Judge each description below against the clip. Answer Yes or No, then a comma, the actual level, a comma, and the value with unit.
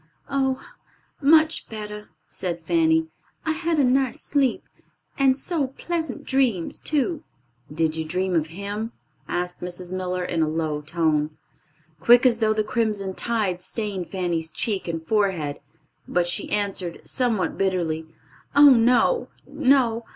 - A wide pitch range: Yes, wide, 7.1 semitones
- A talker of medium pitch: No, high, 210 Hz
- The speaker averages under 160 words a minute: Yes, slow, 135 wpm